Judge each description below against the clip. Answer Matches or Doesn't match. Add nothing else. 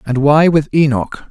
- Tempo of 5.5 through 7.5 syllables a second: Doesn't match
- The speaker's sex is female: Doesn't match